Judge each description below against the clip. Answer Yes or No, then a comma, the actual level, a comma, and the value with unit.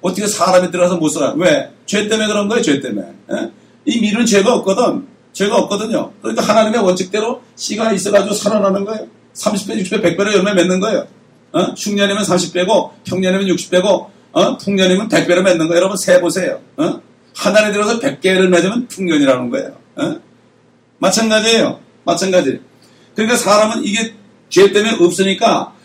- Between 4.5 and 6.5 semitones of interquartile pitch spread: No, average, 3.2 semitones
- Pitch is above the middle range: Yes, high, 205 Hz